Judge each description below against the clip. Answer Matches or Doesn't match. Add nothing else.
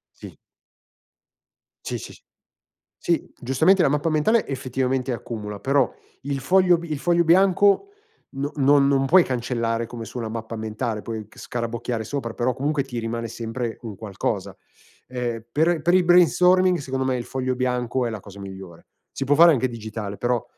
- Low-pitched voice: Matches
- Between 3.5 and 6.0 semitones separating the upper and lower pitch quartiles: Matches